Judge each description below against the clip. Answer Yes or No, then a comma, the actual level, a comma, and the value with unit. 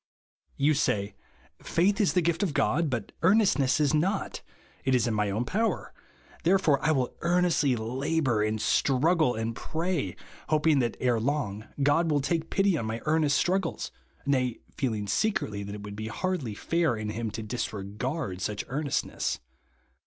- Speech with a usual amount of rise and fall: No, wide, 6.8 semitones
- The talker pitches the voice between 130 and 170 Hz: Yes, medium, 140 Hz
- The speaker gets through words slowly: No, average, 160 wpm